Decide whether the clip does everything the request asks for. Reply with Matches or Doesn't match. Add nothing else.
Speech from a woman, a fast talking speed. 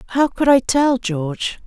Doesn't match